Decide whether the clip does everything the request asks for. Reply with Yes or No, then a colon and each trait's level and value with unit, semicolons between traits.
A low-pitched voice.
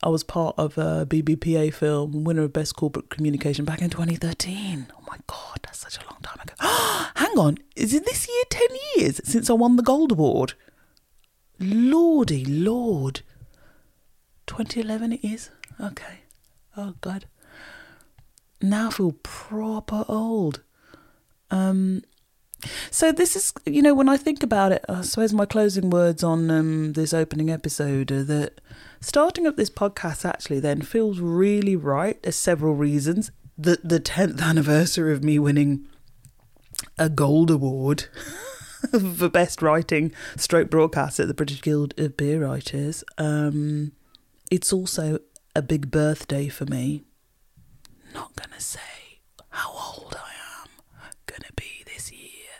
No: medium, 160 Hz